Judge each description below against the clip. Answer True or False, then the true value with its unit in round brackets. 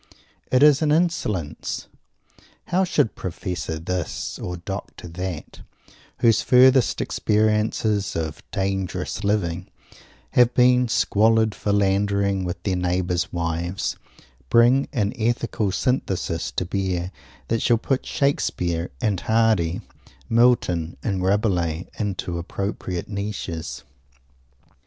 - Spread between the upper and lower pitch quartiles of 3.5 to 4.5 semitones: True (4.2 semitones)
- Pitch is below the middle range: True (100 Hz)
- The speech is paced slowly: True (105 wpm)